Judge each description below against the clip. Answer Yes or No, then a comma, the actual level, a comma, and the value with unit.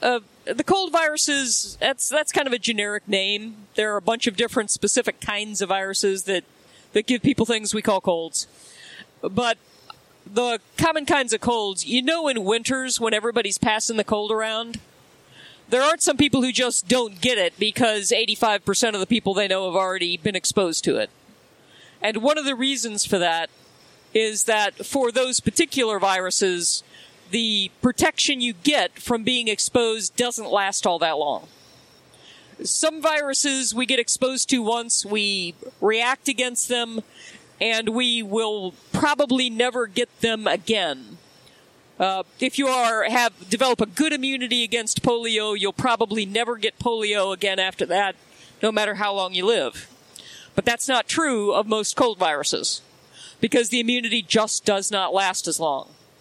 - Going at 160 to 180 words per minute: Yes, average, 165 wpm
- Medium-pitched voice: No, high, 225 Hz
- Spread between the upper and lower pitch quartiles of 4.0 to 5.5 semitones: No, average, 3.4 semitones